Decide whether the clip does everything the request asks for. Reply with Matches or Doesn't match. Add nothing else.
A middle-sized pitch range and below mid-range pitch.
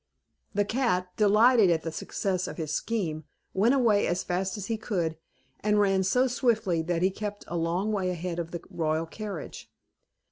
Doesn't match